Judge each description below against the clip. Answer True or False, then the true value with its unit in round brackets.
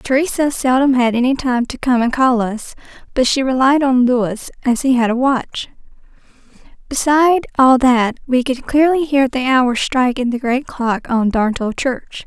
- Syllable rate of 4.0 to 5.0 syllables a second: True (4.7 syllables/s)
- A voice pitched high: True (255 Hz)